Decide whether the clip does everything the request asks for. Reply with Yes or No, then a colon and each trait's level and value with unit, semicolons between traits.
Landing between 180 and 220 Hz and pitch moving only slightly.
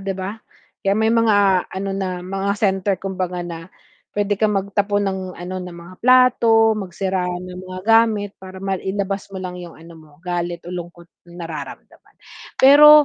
Yes: high, 190 Hz; narrow, 2.3 semitones